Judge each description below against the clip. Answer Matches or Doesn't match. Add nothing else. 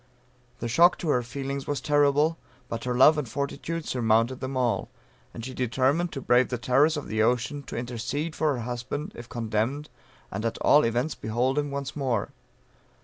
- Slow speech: Doesn't match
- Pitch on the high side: Doesn't match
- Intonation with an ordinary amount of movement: Matches